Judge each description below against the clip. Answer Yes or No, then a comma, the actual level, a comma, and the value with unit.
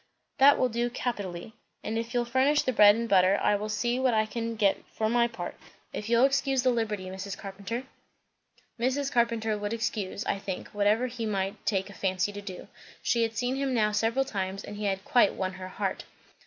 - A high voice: Yes, high, 220 Hz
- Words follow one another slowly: No, fast, 205 wpm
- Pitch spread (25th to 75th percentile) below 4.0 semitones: Yes, average, 3.2 semitones